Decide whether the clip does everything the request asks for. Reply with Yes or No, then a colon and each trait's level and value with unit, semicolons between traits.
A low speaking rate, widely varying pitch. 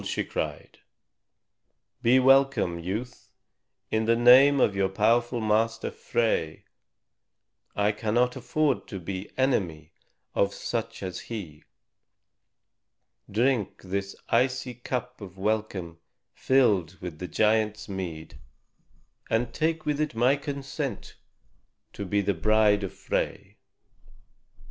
No: slow, 110 wpm; average, 4.4 semitones